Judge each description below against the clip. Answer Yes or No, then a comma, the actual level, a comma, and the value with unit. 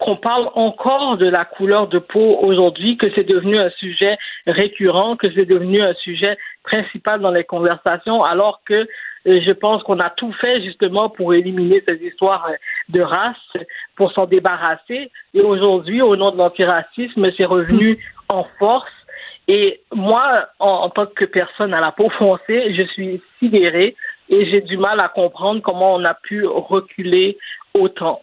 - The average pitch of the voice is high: Yes, high, 200 Hz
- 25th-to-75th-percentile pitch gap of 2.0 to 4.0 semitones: Yes, average, 3.1 semitones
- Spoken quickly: No, average, 165 wpm